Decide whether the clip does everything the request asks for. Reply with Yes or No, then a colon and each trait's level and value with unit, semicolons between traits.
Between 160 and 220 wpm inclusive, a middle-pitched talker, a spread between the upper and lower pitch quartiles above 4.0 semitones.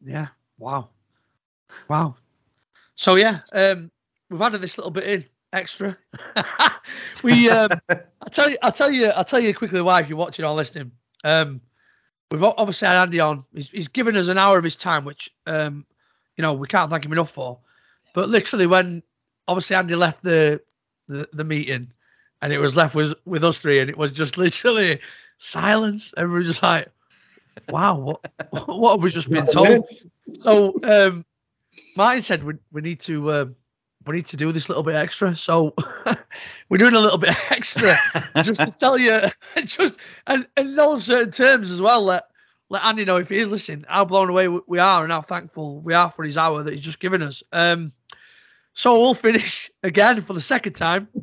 Yes: average, 190 wpm; medium, 175 Hz; average, 5.3 semitones